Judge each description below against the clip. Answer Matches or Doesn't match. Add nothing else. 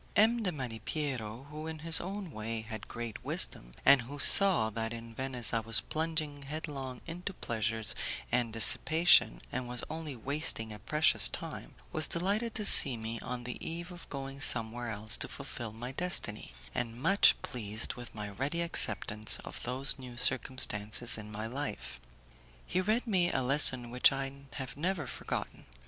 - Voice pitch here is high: Doesn't match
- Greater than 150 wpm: Matches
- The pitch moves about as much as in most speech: Doesn't match